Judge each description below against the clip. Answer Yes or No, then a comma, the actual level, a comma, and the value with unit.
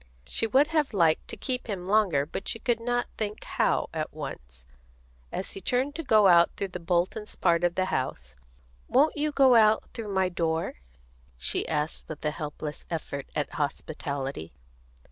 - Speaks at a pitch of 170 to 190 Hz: Yes, medium, 185 Hz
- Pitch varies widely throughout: Yes, wide, 6.9 semitones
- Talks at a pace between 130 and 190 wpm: Yes, average, 175 wpm